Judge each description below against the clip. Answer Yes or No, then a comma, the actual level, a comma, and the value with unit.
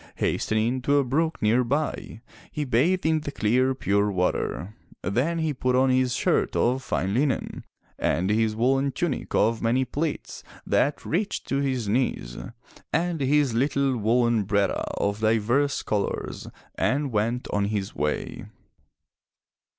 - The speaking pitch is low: Yes, low, 125 Hz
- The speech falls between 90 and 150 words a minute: Yes, average, 140 wpm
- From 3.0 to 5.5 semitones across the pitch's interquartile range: Yes, average, 4.5 semitones